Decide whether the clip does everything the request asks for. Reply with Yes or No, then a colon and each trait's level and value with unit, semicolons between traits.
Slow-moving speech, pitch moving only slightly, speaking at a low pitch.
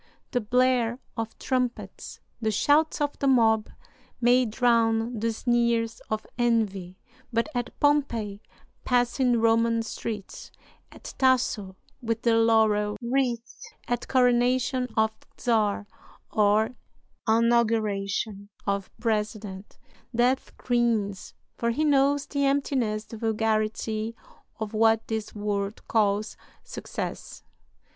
No: slow, 105 wpm; narrow, 2.3 semitones; high, 230 Hz